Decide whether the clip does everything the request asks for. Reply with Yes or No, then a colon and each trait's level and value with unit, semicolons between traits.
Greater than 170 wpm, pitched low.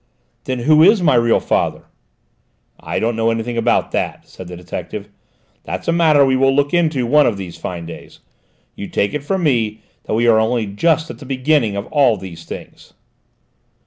Yes: average, 190 wpm; low, 120 Hz